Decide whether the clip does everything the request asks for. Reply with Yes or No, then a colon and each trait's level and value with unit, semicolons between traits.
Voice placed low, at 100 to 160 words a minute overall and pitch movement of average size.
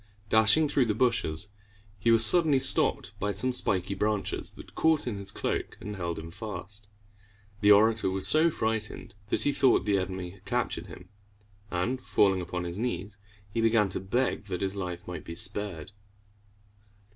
No: low, 105 Hz; average, 170 wpm; average, 3.5 semitones